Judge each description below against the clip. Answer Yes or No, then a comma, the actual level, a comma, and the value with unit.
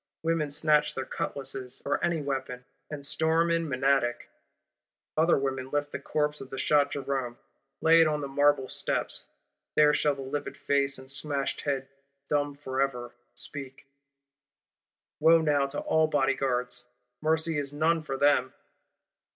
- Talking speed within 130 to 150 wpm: Yes, average, 145 wpm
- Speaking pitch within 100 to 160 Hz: Yes, medium, 140 Hz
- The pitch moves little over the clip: Yes, narrow, 2.1 semitones